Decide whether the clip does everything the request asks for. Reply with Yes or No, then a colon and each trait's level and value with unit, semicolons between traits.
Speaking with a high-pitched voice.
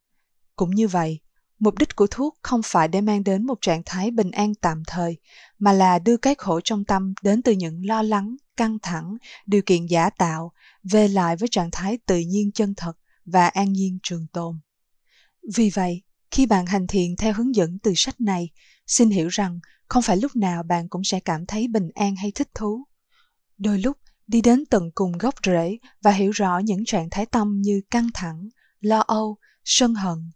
Yes: high, 200 Hz